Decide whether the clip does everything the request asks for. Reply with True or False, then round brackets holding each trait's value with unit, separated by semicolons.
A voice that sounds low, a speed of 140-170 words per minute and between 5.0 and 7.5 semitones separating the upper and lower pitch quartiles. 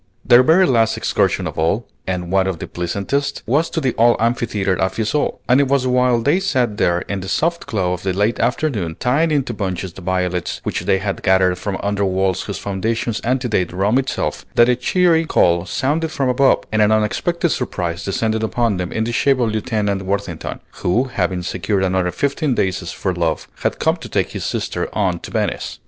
False (110 Hz; 200 wpm; 5.3 semitones)